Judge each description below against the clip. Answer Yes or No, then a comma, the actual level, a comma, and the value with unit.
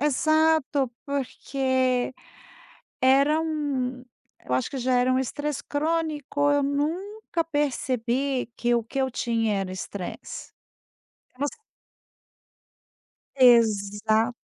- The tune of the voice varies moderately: Yes, average, 3.3 semitones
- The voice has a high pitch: Yes, very high, 265 Hz